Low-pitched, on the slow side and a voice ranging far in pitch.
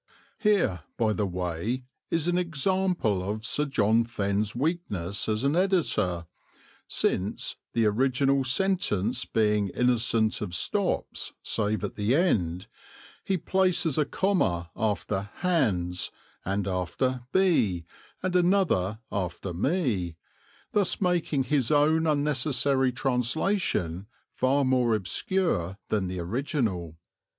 Yes: low, 120 Hz; slow, 115 wpm; wide, 8.1 semitones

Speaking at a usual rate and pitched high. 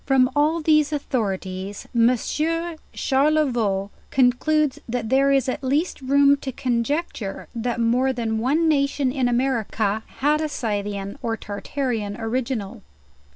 No: slow, 125 wpm; very high, 255 Hz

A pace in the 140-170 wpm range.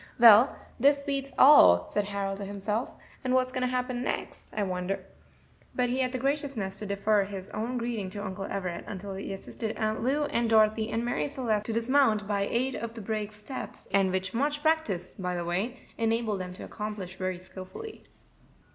No: average, 190 wpm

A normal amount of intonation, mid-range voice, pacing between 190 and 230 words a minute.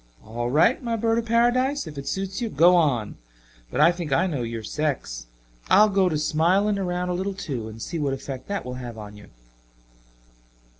No: wide, 7.7 semitones; medium, 165 Hz; average, 200 wpm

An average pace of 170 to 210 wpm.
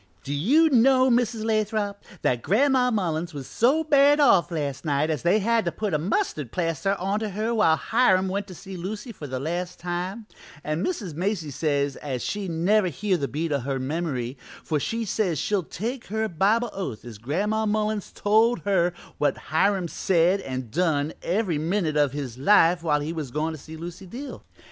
Yes: average, 190 wpm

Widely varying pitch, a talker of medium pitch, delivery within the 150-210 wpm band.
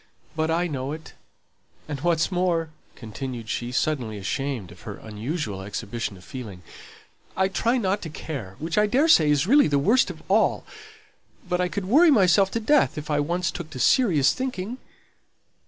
Yes: wide, 6.9 semitones; medium, 160 Hz; average, 170 wpm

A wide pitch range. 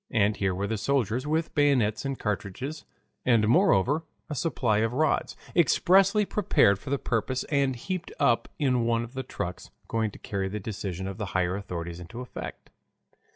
Yes: wide, 5.8 semitones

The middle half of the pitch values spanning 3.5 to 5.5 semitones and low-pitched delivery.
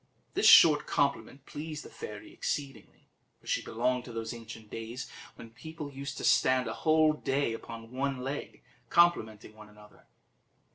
Yes: average, 4.5 semitones; low, 130 Hz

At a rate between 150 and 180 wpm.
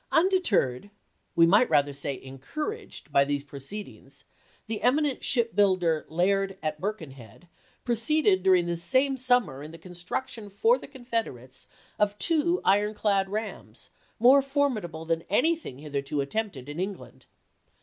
No: average, 140 wpm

